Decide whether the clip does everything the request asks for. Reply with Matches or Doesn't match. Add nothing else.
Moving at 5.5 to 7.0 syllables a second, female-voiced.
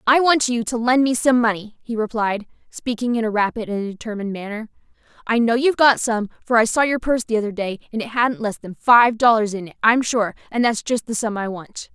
Matches